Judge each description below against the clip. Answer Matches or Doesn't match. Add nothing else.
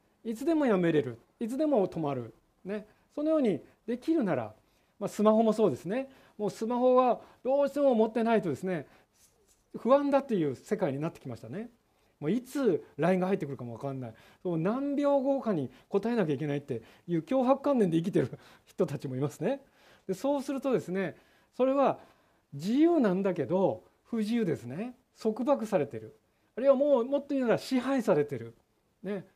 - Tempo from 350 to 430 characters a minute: Matches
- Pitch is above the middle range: Matches